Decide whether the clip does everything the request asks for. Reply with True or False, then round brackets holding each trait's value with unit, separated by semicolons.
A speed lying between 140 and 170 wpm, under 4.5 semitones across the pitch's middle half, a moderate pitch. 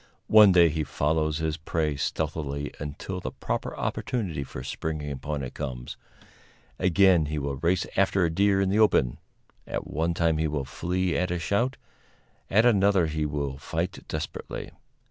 False (165 wpm; 4.1 semitones; 80 Hz)